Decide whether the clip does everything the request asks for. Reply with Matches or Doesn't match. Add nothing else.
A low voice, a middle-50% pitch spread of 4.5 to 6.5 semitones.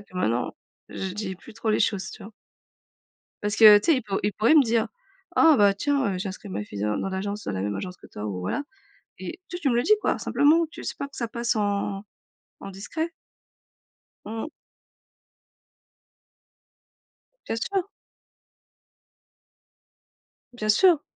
Doesn't match